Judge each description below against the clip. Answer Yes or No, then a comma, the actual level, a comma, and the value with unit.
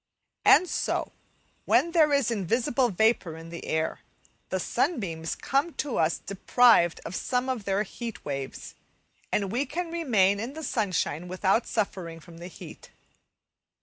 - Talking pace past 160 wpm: No, average, 150 wpm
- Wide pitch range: Yes, wide, 6.8 semitones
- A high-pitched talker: Yes, high, 210 Hz